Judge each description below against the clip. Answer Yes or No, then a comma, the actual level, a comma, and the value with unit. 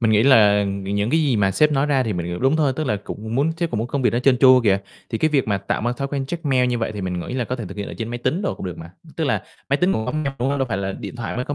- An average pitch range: Yes, average, 5.0 semitones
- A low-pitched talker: Yes, low, 120 Hz